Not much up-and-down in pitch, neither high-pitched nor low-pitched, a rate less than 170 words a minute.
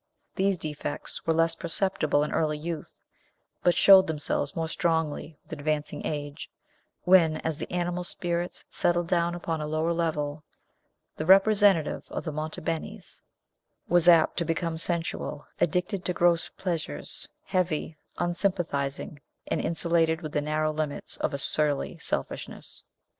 Yes: narrow, 2.3 semitones; medium, 165 Hz; average, 140 wpm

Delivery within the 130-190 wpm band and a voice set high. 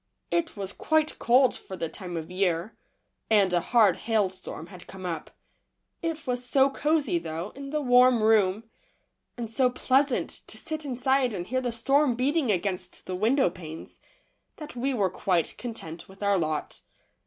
Yes: average, 165 wpm; high, 225 Hz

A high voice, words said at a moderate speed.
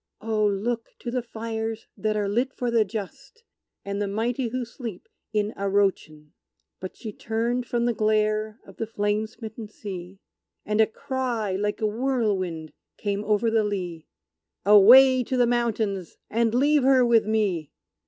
Yes: high, 220 Hz; average, 160 wpm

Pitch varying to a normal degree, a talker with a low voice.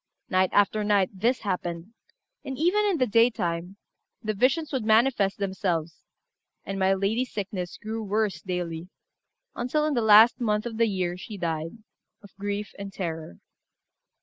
No: average, 3.7 semitones; high, 205 Hz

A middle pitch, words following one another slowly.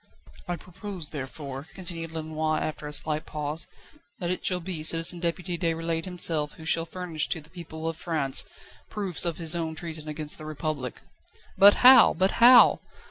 No: medium, 165 Hz; average, 170 wpm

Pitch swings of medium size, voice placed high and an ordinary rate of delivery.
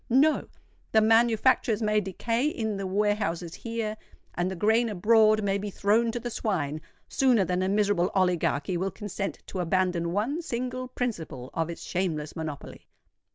Yes: average, 4.1 semitones; high, 205 Hz; average, 155 wpm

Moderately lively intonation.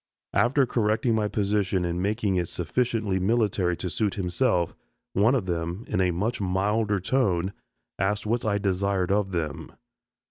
Yes: average, 3.1 semitones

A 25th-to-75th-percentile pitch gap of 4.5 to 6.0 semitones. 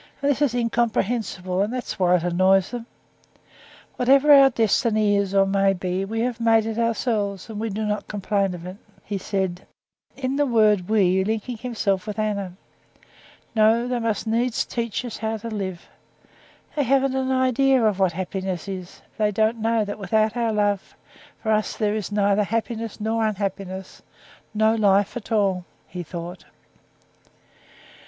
No: average, 3.1 semitones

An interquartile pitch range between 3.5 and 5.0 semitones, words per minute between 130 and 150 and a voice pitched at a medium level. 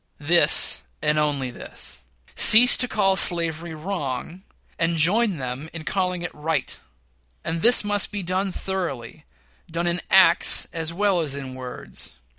Yes: average, 4.0 semitones; average, 145 wpm; medium, 170 Hz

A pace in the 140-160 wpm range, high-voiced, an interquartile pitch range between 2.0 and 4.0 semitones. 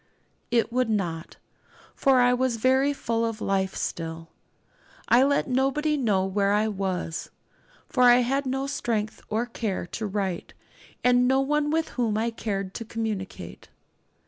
No: average, 150 wpm; high, 230 Hz; average, 4.6 semitones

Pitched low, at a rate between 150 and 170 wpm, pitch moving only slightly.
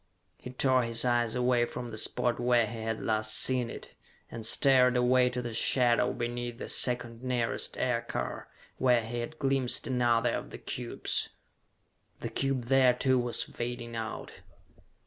Yes: low, 120 Hz; average, 160 wpm; narrow, 1.3 semitones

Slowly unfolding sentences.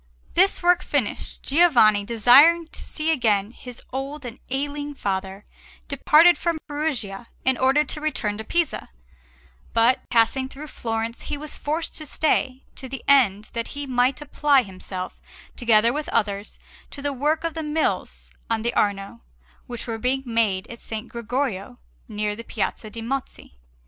No: average, 160 wpm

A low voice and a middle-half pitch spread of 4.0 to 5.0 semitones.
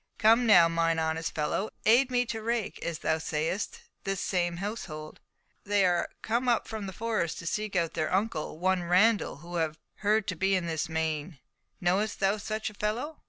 No: high, 190 Hz; average, 4.6 semitones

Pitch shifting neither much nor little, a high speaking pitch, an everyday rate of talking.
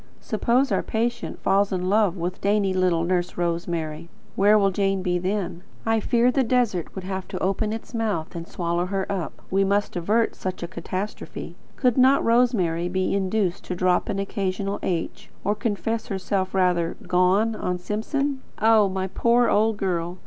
Yes: average, 3.3 semitones; high, 195 Hz; average, 180 wpm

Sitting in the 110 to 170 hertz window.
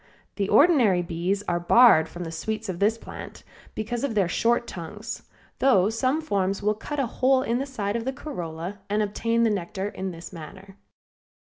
No: high, 205 Hz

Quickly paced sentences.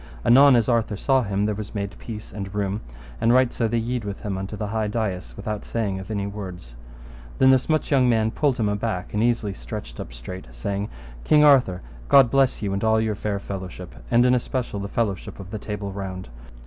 Yes: fast, 215 wpm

